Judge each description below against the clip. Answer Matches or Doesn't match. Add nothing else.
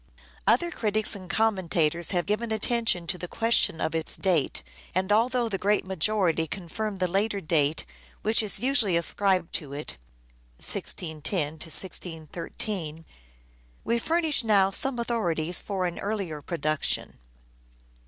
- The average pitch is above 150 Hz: Matches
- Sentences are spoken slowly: Matches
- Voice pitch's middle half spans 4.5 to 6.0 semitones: Matches